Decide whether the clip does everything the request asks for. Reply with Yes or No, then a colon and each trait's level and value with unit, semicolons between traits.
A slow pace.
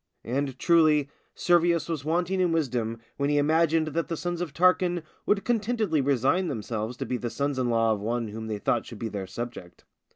No: average, 200 wpm